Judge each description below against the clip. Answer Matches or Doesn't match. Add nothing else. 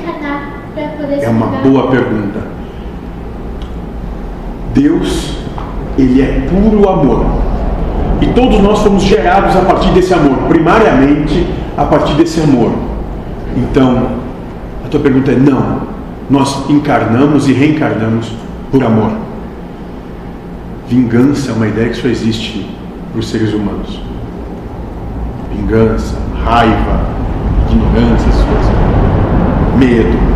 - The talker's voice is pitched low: Matches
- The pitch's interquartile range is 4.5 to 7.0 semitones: Matches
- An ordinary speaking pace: Doesn't match